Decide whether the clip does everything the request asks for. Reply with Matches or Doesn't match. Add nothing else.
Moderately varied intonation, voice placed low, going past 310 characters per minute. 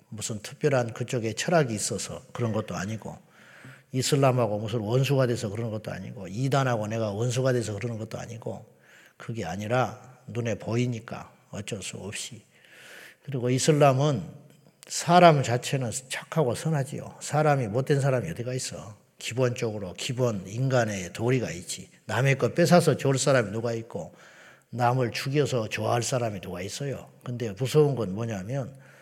Matches